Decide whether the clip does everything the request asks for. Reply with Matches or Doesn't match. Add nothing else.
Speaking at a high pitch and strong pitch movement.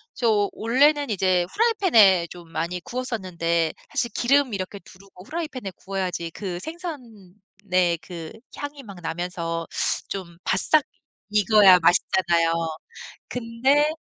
Matches